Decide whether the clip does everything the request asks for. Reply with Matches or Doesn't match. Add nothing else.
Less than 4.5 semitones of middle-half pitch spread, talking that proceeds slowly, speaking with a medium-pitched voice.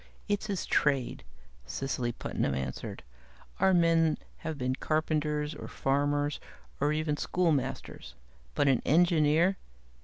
Matches